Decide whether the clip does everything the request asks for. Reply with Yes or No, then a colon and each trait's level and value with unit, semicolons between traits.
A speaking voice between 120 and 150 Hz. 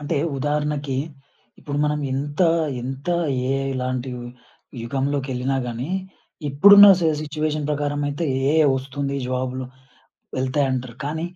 Yes: medium, 140 Hz